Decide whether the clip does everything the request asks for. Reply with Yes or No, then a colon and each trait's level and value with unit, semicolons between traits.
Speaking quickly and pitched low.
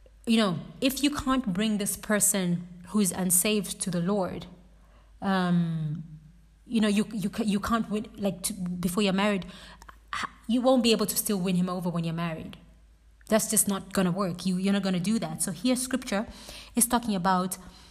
No: fast, 220 wpm; high, 200 Hz